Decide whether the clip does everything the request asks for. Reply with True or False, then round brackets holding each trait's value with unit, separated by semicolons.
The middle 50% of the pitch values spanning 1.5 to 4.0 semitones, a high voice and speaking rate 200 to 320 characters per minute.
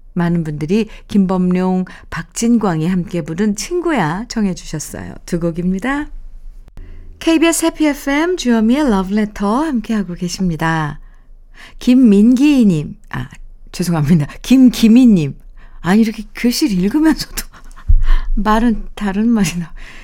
False (5.4 semitones; 205 Hz; 260 characters per minute)